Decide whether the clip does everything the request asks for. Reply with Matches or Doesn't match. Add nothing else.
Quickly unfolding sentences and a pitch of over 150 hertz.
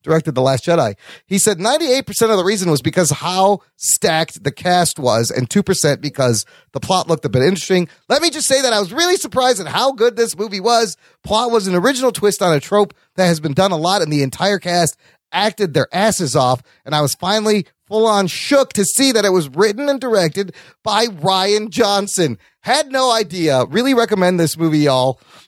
Matches